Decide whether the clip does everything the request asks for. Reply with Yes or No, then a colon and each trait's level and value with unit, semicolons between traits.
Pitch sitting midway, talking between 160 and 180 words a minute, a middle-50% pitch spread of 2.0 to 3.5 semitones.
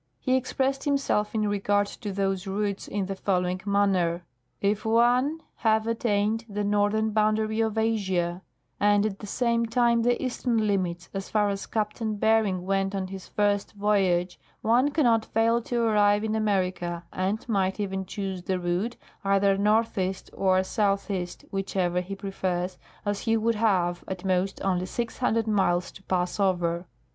No: high, 205 Hz; average, 165 wpm; average, 2.7 semitones